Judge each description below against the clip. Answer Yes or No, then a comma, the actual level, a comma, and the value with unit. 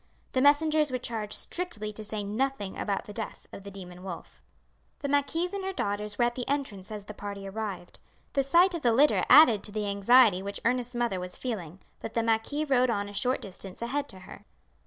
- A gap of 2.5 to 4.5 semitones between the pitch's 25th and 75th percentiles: No, average, 5.1 semitones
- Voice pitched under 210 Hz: No, high, 225 Hz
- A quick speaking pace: Yes, fast, 215 wpm